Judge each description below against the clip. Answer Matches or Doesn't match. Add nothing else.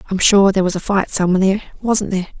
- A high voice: Matches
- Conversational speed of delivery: Doesn't match